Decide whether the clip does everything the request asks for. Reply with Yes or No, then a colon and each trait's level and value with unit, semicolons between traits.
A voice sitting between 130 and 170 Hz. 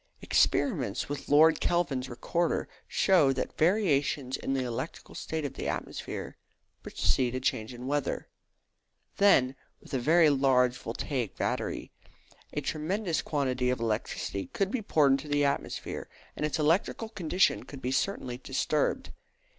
Yes: medium, 140 Hz